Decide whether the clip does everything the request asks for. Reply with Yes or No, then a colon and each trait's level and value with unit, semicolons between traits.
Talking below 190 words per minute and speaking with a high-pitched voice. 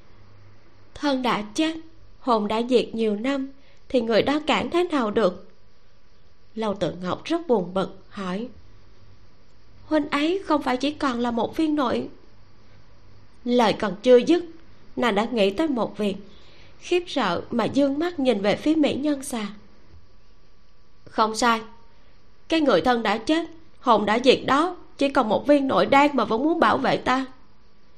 Yes: slow, 165 wpm; high, 230 Hz